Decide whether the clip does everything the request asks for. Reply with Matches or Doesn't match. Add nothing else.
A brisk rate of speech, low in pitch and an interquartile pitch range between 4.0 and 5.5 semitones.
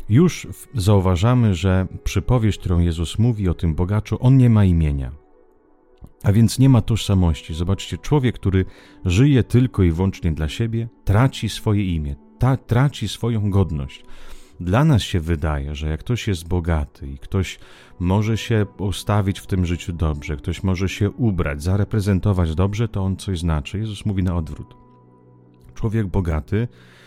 Doesn't match